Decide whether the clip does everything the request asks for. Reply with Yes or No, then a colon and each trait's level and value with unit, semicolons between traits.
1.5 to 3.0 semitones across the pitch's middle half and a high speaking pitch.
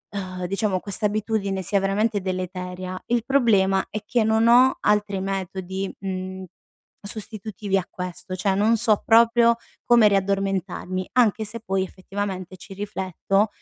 Yes: narrow, 2.4 semitones; high, 195 Hz